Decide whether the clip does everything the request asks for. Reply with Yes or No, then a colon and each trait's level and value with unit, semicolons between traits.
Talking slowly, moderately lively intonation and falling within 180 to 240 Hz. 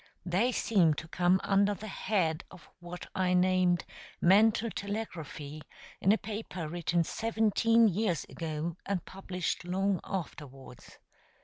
Yes: slow, 125 wpm; average, 3.4 semitones; medium, 185 Hz